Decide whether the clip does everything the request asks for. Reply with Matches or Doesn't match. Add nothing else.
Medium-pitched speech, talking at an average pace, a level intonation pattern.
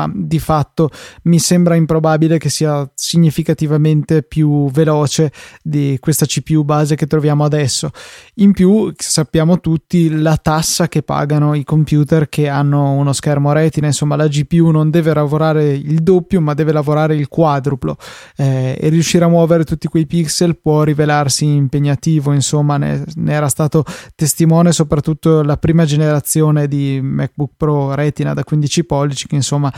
Matches